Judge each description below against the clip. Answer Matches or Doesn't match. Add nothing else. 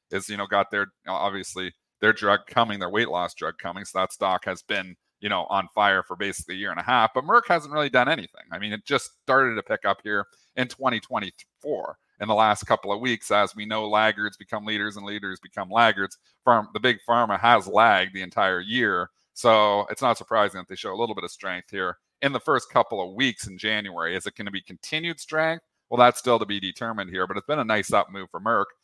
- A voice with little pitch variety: Doesn't match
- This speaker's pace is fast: Matches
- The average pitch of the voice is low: Matches